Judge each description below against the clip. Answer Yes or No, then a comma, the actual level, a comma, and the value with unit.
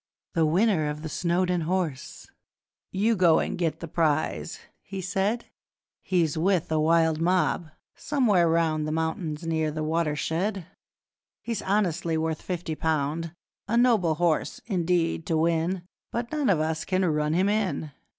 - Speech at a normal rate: Yes, average, 150 wpm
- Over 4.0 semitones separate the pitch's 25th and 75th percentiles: No, average, 3.0 semitones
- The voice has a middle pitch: Yes, medium, 165 Hz